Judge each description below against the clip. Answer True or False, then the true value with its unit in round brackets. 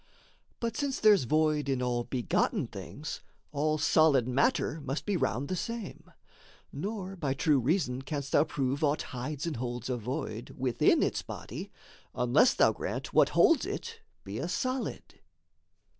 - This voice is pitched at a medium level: True (145 Hz)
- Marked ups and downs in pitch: True (6.1 semitones)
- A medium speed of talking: True (155 wpm)